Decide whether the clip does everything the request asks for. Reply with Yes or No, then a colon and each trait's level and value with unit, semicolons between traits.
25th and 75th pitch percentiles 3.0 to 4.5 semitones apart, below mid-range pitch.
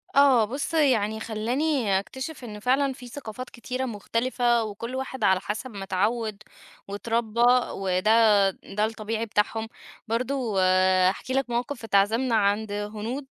No: average, 3.4 semitones; high, 225 Hz